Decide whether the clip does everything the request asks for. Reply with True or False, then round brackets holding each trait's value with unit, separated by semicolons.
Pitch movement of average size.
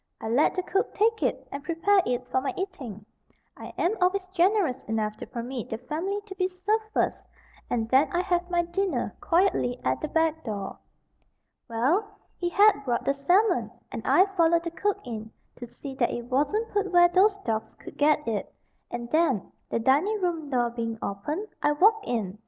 False (7.6 semitones)